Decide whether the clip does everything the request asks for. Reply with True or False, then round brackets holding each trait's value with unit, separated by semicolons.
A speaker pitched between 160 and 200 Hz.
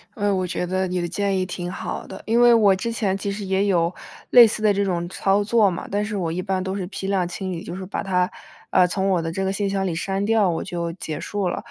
True (190 Hz)